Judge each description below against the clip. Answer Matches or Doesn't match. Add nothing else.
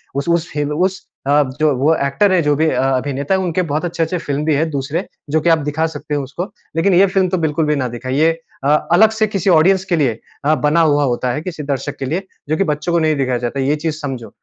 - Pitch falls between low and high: Matches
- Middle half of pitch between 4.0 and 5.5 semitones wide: Doesn't match